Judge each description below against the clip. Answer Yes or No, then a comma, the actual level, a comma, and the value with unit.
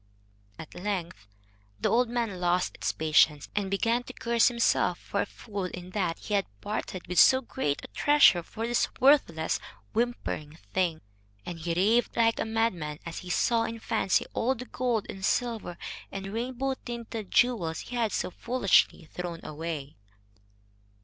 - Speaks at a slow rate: No, average, 160 wpm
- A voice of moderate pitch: No, high, 200 Hz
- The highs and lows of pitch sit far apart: Yes, wide, 5.7 semitones